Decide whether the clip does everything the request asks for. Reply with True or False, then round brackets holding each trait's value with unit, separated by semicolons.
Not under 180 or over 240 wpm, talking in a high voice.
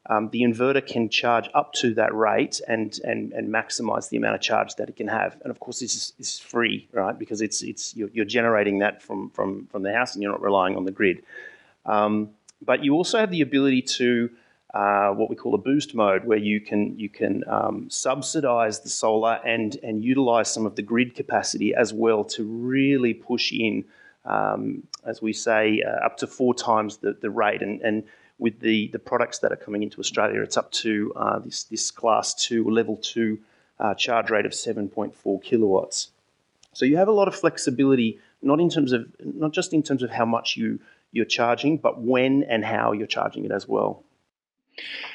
False (205 wpm; 115 Hz)